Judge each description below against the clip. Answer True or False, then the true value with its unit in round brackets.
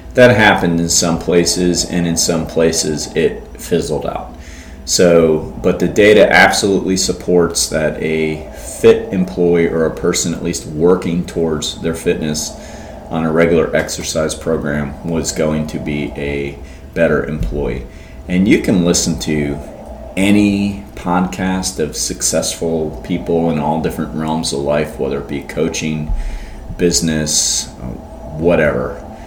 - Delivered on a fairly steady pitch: True (2.3 semitones)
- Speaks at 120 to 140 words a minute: True (135 wpm)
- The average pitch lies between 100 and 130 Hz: False (80 Hz)